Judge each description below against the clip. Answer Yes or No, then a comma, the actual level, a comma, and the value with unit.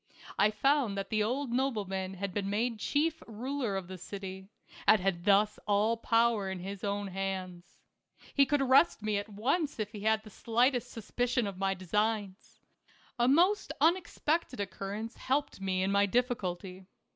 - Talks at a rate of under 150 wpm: No, average, 170 wpm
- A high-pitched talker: Yes, high, 210 Hz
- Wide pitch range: No, average, 4.2 semitones